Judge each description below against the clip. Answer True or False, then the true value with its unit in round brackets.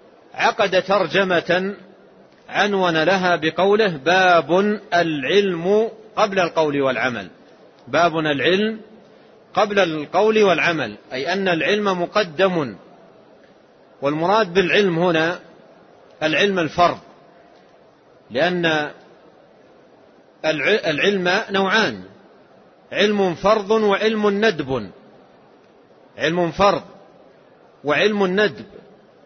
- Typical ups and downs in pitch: True (3.4 semitones)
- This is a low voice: False (185 Hz)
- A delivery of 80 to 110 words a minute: False (70 wpm)